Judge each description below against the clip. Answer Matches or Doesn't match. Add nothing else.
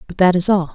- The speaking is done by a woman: Matches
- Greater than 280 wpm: Matches